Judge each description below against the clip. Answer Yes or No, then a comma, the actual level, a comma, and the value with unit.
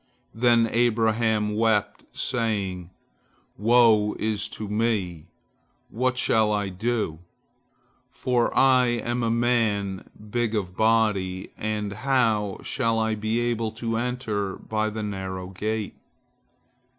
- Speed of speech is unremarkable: No, slow, 110 wpm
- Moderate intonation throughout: No, narrow, 2.3 semitones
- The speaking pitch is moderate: No, low, 110 Hz